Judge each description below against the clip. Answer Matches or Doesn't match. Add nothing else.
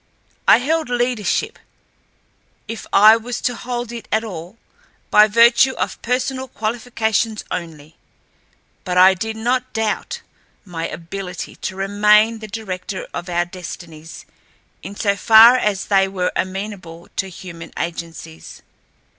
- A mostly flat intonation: Doesn't match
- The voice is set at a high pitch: Matches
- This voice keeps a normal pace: Doesn't match